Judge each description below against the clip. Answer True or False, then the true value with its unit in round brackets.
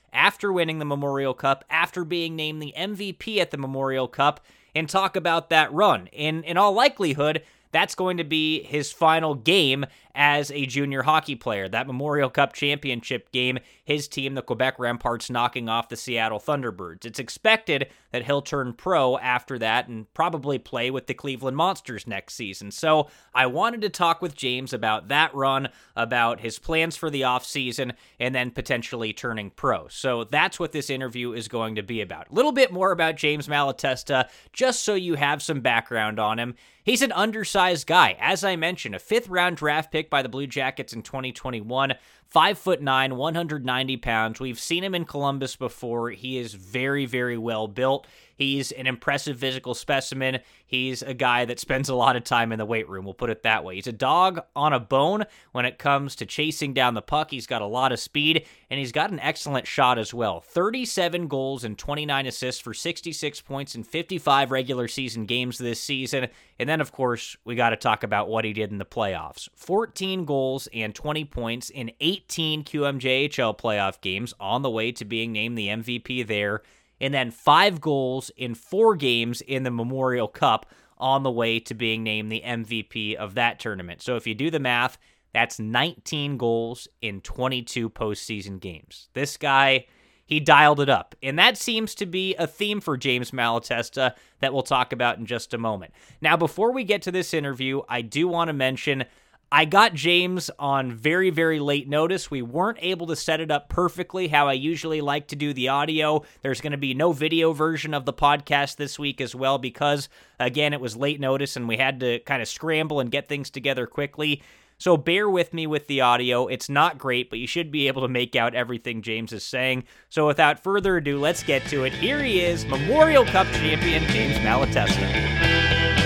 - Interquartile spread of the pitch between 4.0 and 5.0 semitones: True (4.4 semitones)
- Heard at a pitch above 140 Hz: False (135 Hz)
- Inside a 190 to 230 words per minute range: True (195 wpm)